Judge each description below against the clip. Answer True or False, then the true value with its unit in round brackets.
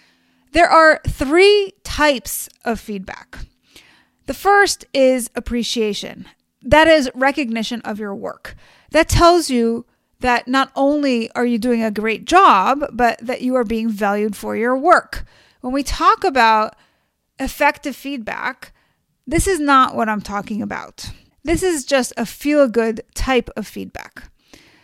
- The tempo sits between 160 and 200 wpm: False (145 wpm)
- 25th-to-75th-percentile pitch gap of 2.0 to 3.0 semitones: False (4.6 semitones)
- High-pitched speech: True (255 Hz)